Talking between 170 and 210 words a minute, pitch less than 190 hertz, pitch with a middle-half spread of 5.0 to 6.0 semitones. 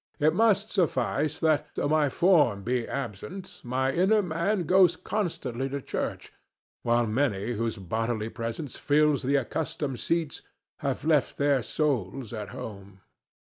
No: average, 140 wpm; medium, 140 Hz; wide, 5.6 semitones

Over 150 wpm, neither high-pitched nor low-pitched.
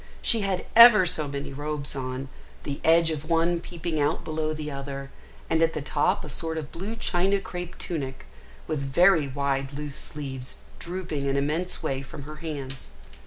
Yes: average, 175 wpm; medium, 150 Hz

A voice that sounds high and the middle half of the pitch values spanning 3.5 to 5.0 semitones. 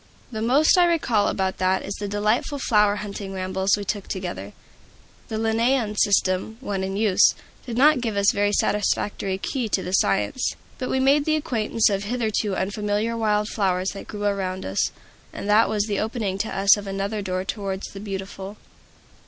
No: high, 205 Hz; narrow, 2.5 semitones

